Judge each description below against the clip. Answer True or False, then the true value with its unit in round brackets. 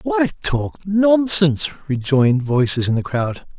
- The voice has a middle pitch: True (150 Hz)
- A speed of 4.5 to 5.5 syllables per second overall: False (4.1 syllables/s)